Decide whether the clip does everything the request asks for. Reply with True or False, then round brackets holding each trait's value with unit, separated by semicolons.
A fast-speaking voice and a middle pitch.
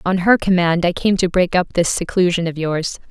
True (230 wpm; 175 Hz)